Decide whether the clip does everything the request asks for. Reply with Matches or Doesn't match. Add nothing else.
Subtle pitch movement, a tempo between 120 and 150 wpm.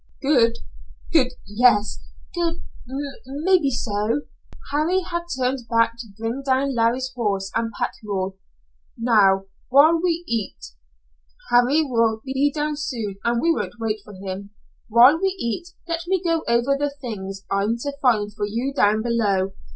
Doesn't match